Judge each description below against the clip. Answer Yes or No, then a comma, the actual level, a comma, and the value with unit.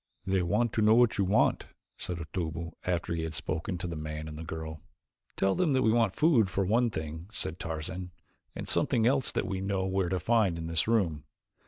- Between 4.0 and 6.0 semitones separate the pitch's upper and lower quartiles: Yes, average, 5.0 semitones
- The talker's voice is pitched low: Yes, very low, 90 Hz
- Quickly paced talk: Yes, fast, 215 wpm